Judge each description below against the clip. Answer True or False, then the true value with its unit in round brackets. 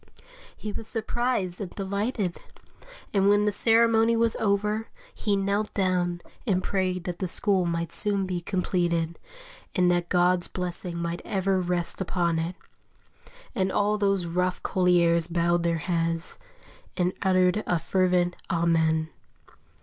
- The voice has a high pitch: False (180 Hz)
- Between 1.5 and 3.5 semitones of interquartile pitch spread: True (2.6 semitones)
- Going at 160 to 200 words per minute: False (135 wpm)